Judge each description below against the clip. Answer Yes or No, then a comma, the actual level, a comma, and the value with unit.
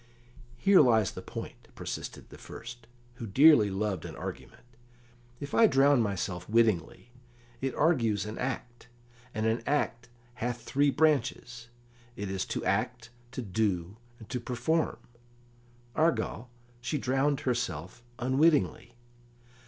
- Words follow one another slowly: Yes, slow, 125 wpm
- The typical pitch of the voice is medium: No, low, 120 Hz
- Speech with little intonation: No, average, 4.2 semitones